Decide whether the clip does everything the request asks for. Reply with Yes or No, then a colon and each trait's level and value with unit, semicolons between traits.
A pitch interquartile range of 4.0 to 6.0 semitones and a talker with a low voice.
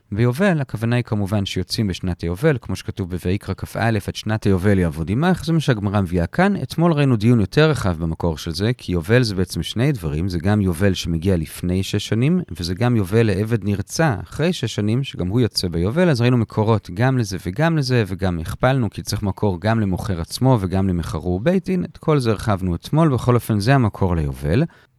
Yes: average, 5.3 semitones; low, 105 Hz